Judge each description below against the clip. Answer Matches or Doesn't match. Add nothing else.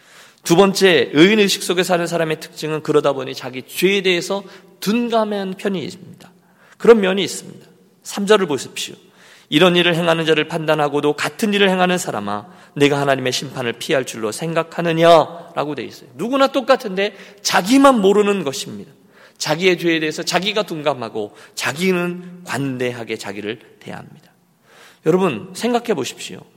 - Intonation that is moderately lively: Matches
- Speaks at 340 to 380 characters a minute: Matches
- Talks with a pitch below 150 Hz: Doesn't match